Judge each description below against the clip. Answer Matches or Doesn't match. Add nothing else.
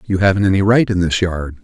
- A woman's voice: Doesn't match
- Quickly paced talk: Matches